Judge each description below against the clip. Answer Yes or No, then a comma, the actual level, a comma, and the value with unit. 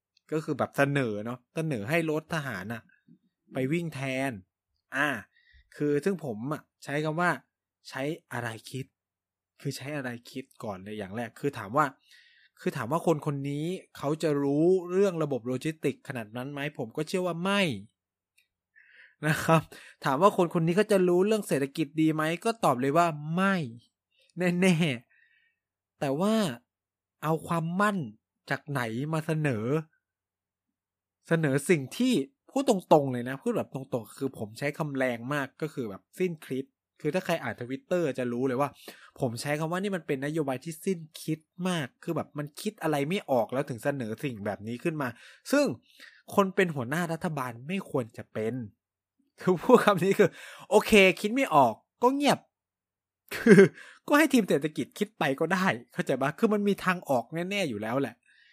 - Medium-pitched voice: Yes, medium, 150 Hz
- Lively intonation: Yes, wide, 5.9 semitones